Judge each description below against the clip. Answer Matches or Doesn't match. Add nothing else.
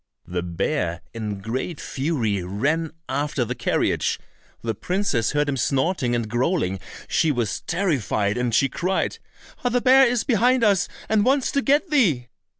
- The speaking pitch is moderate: Matches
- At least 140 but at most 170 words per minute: Matches